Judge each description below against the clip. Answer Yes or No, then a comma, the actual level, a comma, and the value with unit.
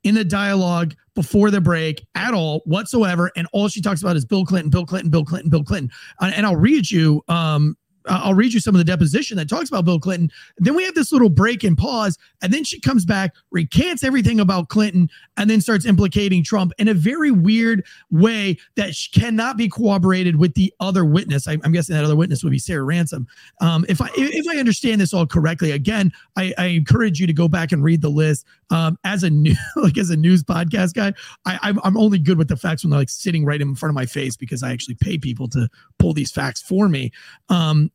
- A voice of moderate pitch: Yes, medium, 180 Hz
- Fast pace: Yes, fast, 230 wpm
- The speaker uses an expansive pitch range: No, average, 4.2 semitones